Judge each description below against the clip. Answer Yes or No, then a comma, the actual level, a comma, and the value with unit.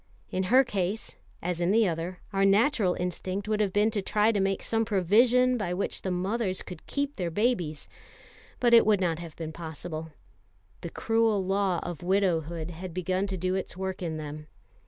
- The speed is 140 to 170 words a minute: No, average, 190 wpm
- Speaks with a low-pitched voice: No, high, 190 Hz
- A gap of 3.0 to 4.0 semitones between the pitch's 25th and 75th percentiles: Yes, average, 3.4 semitones